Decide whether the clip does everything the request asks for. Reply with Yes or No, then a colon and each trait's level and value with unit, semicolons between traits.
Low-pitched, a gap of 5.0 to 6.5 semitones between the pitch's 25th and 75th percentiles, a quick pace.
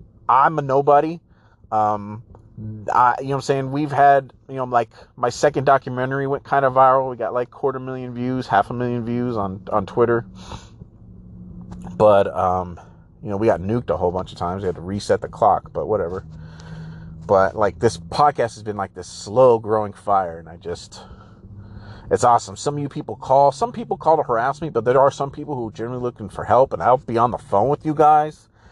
Yes: low, 115 Hz; wide, 5.5 semitones; fast, 215 wpm